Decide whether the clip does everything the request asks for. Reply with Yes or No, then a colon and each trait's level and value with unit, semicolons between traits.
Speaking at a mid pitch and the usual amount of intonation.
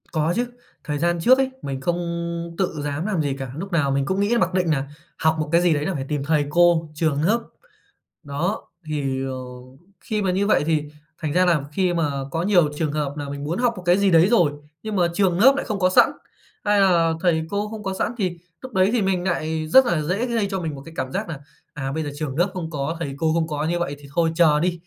Yes: medium, 170 Hz; average, 4.2 semitones